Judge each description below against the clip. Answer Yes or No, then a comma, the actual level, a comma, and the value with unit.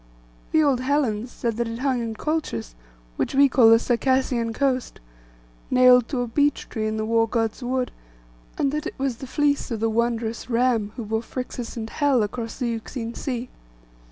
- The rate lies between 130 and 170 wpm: No, average, 185 wpm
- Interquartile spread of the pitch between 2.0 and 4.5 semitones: Yes, narrow, 2.6 semitones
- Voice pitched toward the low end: No, high, 245 Hz